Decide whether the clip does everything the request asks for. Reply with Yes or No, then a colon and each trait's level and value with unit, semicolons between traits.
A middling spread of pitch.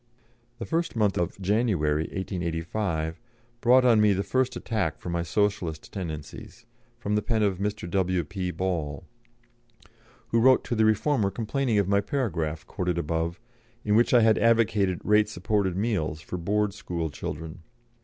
Yes: average, 4.2 semitones